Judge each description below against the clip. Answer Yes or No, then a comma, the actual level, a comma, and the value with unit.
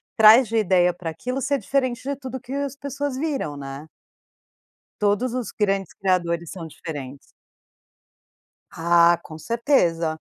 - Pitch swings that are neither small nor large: No, wide, 7.5 semitones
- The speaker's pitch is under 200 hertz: No, high, 205 Hz